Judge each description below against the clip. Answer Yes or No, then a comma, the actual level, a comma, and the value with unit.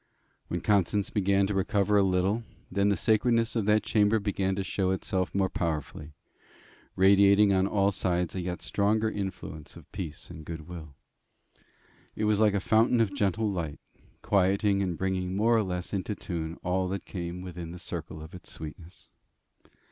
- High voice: No, very low, 95 Hz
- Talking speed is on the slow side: No, average, 170 wpm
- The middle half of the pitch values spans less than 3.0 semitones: Yes, narrow, 2.5 semitones